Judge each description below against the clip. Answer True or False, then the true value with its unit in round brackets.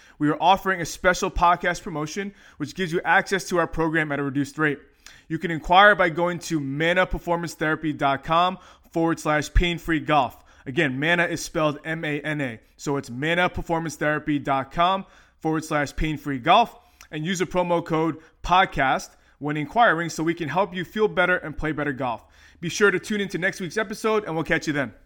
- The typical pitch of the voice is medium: True (165 Hz)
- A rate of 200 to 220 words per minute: False (180 wpm)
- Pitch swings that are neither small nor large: True (3.2 semitones)